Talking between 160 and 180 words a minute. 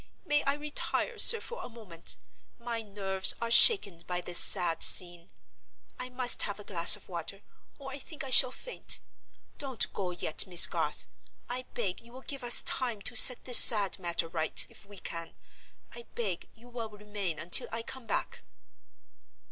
Yes: average, 175 wpm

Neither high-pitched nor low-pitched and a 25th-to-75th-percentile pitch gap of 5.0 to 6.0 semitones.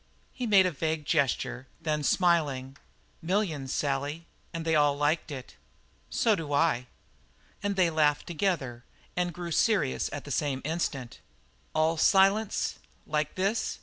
No: medium, 160 Hz; average, 3.8 semitones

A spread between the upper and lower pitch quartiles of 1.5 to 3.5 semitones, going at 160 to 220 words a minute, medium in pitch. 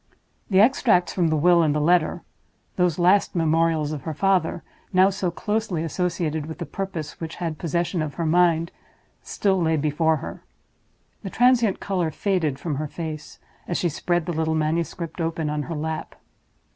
Yes: narrow, 2.4 semitones; average, 165 wpm; medium, 165 Hz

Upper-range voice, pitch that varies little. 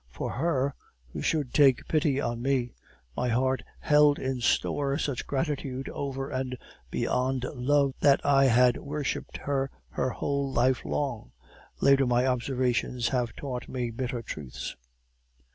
No: low, 130 Hz; narrow, 2.1 semitones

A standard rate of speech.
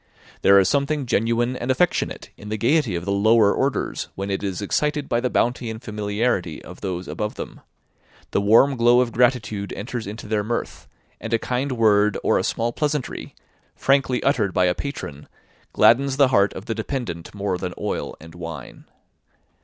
Yes: average, 180 wpm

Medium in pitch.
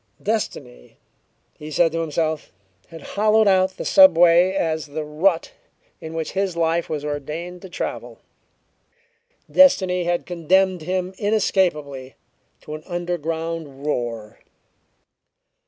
Yes: medium, 165 Hz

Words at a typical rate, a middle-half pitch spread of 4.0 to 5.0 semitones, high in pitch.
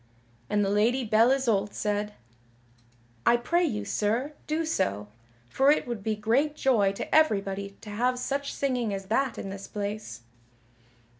Yes: average, 155 wpm; average, 4.6 semitones; high, 220 Hz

